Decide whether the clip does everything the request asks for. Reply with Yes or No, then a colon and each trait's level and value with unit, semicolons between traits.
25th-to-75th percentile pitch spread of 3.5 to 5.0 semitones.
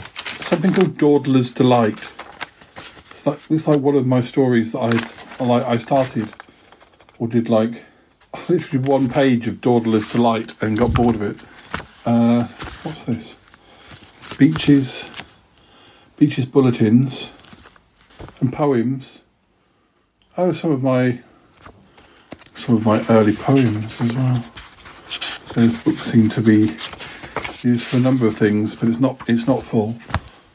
No: average, 2.8 semitones